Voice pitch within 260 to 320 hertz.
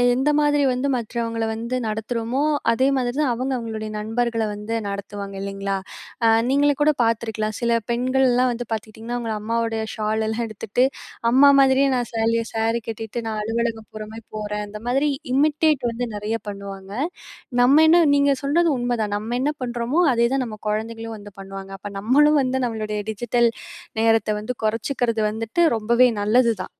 No: high, 230 Hz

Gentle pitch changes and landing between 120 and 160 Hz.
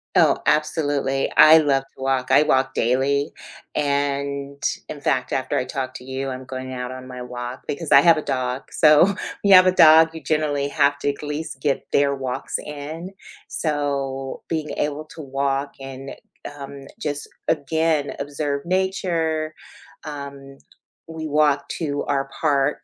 Yes: narrow, 2.2 semitones; medium, 140 Hz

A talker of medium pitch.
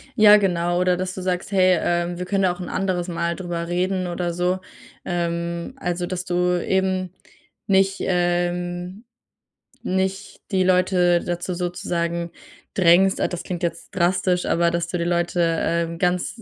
Yes: medium, 180 Hz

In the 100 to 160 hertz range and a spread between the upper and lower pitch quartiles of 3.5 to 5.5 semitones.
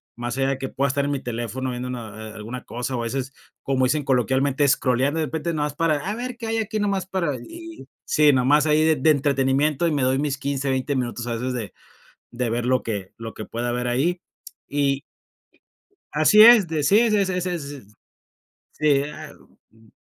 Yes: medium, 140 Hz; average, 3.9 semitones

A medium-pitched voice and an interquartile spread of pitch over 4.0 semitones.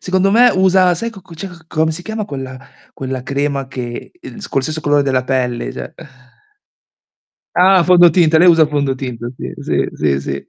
Yes: medium, 155 Hz; wide, 5.6 semitones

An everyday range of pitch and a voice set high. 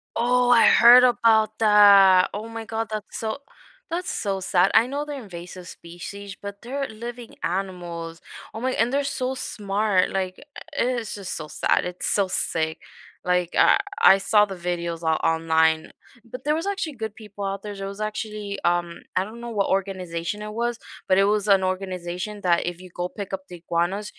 Yes: average, 3.7 semitones; high, 200 Hz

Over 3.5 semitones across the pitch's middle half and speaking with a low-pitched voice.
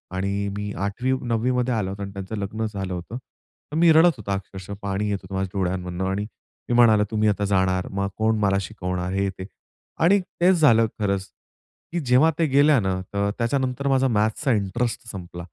Yes: average, 4.2 semitones; low, 105 Hz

